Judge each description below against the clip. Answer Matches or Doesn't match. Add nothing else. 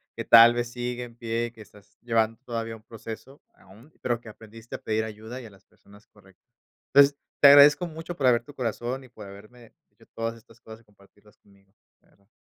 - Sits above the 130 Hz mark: Doesn't match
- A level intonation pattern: Matches